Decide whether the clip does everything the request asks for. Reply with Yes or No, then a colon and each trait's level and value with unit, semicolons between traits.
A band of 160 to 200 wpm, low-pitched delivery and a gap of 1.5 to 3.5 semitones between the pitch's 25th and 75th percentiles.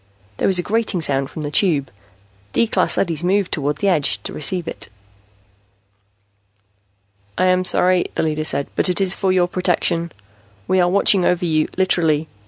No: average, 175 wpm; medium, 175 Hz; average, 3.2 semitones